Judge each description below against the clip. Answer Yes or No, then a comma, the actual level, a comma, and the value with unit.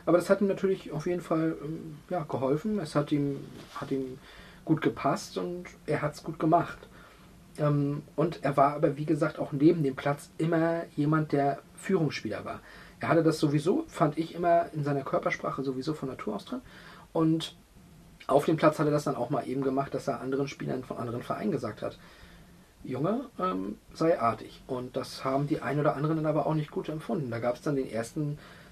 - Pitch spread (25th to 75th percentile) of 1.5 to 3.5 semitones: Yes, average, 3.2 semitones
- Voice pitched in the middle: Yes, medium, 150 Hz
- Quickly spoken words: Yes, fast, 205 wpm